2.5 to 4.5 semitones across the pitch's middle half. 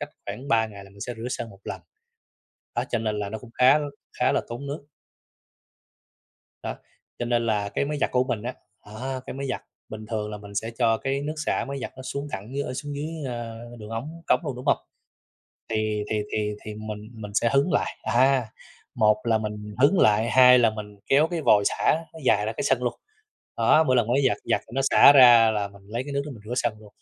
Yes: average, 3.9 semitones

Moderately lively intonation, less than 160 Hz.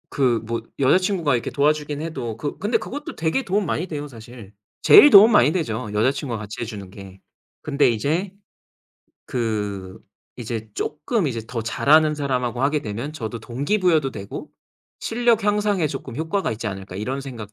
No: wide, 6.1 semitones; low, 135 Hz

